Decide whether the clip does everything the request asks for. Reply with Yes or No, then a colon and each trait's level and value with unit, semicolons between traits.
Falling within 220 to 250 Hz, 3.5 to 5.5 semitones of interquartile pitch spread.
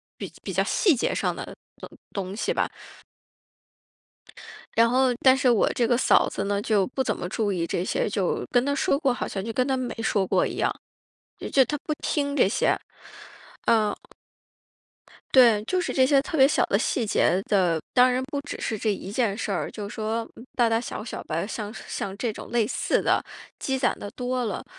Yes: high, 230 Hz; average, 4.2 semitones